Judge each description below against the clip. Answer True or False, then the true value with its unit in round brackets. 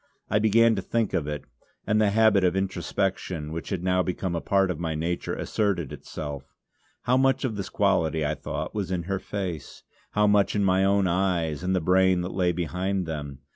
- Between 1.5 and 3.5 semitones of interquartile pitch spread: True (3.2 semitones)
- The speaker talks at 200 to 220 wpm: True (205 wpm)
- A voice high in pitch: False (95 Hz)